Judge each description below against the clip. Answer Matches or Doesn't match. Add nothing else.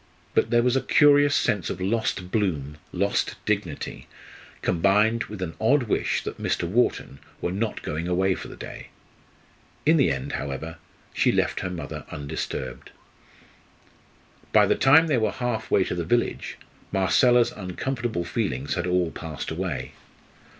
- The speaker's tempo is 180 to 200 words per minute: Doesn't match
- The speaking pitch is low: Matches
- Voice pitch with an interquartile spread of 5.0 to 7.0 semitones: Matches